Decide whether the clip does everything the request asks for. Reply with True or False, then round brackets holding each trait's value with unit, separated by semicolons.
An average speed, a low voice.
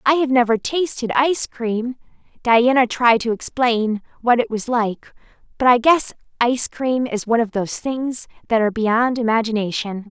False (165 wpm; 235 Hz)